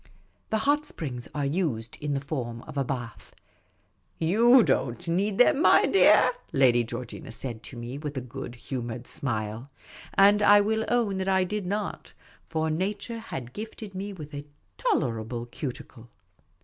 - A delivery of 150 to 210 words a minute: Yes, average, 160 wpm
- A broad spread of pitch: Yes, wide, 9.0 semitones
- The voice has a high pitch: No, medium, 150 Hz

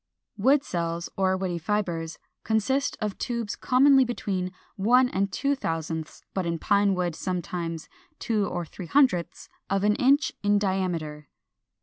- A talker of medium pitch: No, high, 195 Hz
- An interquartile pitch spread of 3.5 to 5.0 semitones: Yes, average, 4.7 semitones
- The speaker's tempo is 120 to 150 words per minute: Yes, average, 145 wpm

